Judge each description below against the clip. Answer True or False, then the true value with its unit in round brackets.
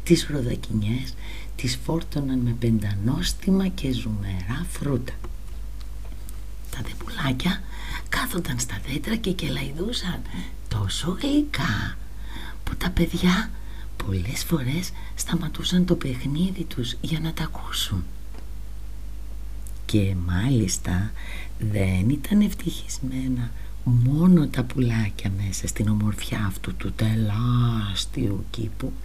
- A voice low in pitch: True (120 Hz)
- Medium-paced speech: False (95 wpm)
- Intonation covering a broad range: True (7.3 semitones)